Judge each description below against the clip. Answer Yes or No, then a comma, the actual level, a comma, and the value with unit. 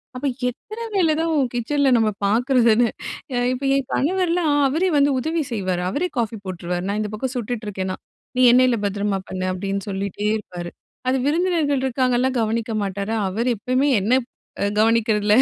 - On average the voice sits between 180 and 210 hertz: No, high, 235 Hz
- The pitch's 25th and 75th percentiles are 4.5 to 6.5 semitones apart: Yes, average, 5.2 semitones